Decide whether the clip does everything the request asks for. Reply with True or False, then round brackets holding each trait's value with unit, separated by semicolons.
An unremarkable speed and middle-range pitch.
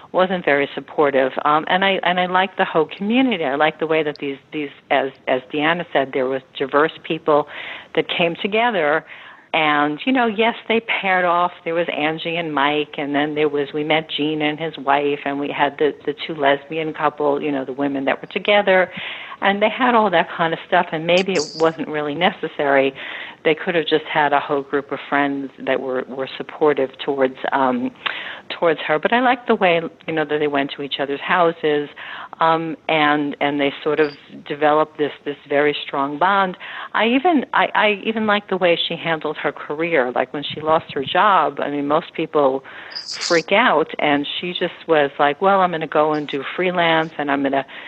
False (210 wpm; 155 Hz)